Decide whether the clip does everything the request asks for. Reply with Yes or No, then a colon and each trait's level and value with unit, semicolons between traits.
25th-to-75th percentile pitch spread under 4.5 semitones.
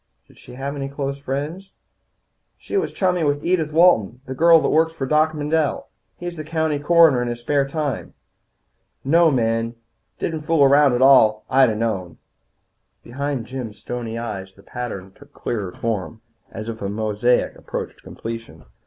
No: average, 5.2 semitones